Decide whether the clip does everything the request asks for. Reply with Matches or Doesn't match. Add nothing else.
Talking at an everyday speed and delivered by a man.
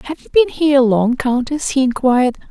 Doesn't match